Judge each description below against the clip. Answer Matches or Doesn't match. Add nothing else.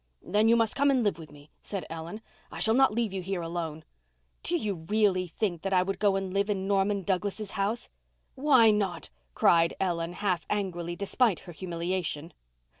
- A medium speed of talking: Matches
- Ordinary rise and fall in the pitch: Matches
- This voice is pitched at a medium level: Doesn't match